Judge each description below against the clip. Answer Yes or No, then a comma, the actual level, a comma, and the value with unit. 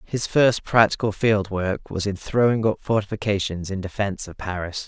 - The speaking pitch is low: Yes, low, 100 Hz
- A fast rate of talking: No, average, 170 wpm